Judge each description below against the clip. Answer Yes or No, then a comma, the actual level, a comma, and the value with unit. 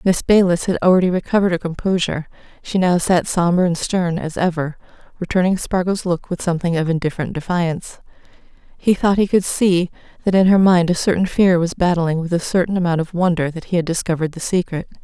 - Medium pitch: Yes, medium, 175 Hz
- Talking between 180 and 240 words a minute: Yes, average, 195 wpm